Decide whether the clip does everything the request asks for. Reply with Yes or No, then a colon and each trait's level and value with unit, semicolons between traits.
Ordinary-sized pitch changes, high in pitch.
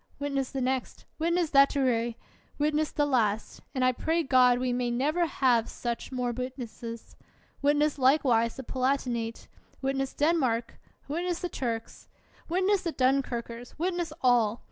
Yes: average, 3.7 semitones; very high, 260 Hz